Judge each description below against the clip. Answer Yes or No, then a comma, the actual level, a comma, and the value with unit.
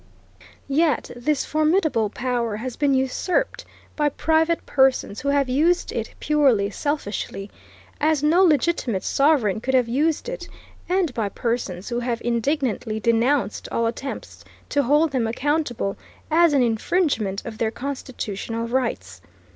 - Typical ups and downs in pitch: Yes, average, 4.7 semitones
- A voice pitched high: Yes, very high, 260 Hz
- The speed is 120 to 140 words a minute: Yes, slow, 135 wpm